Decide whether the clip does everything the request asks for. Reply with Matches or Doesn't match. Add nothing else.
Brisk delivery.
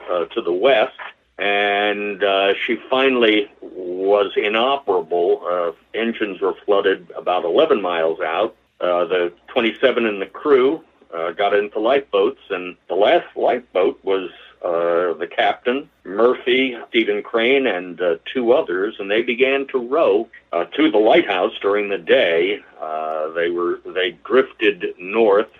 Doesn't match